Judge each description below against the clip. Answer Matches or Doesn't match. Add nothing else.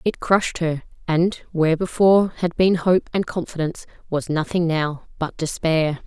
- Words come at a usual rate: Matches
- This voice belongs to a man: Doesn't match